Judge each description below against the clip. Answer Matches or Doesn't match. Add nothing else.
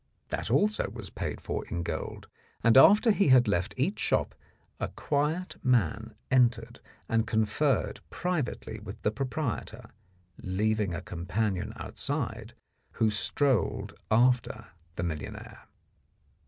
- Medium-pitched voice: Doesn't match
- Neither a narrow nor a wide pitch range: Matches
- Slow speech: Matches